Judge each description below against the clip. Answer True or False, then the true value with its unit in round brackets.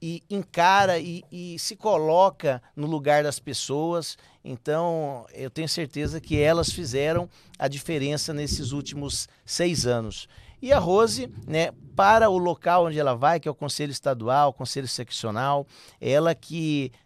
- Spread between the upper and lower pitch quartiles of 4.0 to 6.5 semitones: False (3.6 semitones)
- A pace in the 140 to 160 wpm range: True (150 wpm)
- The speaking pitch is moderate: True (150 Hz)